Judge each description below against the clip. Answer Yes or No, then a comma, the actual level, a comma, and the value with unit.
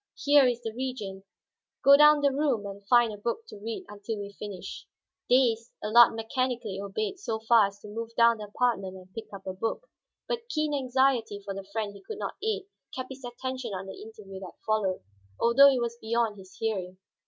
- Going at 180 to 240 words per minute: Yes, average, 200 wpm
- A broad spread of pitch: No, average, 4.2 semitones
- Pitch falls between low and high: No, high, 225 Hz